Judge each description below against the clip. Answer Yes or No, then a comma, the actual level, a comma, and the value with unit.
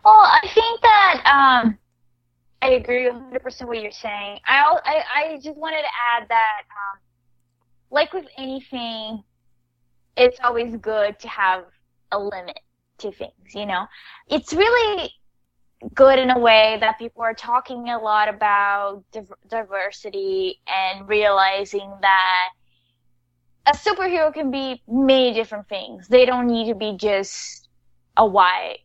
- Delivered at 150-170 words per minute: No, average, 140 wpm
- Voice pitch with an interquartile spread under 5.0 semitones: No, average, 5.3 semitones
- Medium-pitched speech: No, high, 225 Hz